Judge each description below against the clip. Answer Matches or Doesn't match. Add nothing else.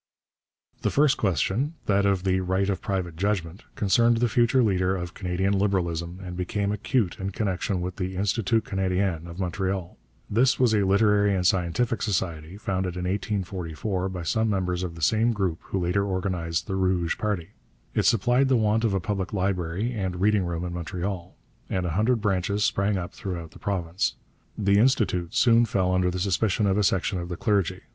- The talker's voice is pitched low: Matches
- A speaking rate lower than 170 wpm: Doesn't match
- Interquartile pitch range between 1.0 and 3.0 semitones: Matches